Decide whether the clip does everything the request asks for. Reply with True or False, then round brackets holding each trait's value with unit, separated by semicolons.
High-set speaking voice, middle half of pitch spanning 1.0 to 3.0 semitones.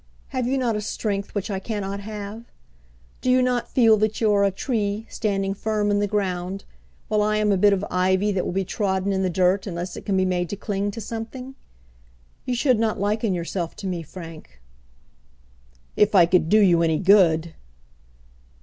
True (200 Hz; 2.5 semitones)